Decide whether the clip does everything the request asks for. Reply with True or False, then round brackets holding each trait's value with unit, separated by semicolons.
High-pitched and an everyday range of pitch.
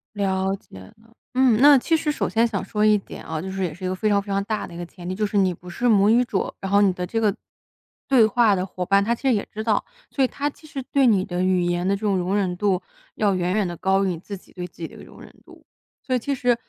True (200 Hz; 3.6 semitones)